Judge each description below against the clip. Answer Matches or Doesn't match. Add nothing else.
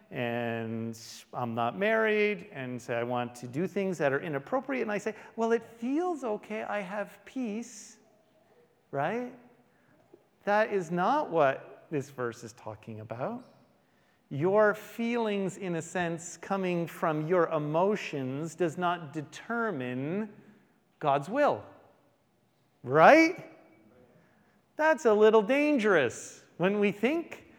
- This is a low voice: Doesn't match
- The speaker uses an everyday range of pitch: Doesn't match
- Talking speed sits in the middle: Doesn't match